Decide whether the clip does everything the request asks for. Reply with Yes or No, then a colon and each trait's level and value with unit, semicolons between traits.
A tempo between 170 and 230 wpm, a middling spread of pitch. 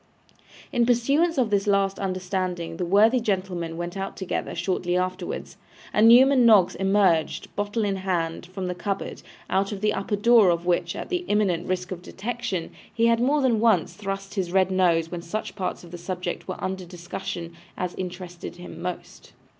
Yes: average, 180 wpm; average, 3.1 semitones